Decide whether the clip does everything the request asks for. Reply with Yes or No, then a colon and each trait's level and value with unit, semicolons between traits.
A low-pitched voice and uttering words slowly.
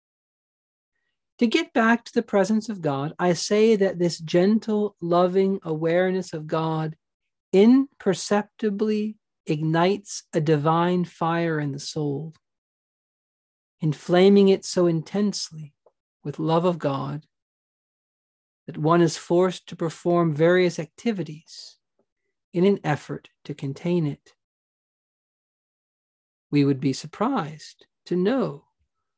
No: medium, 175 Hz; slow, 110 wpm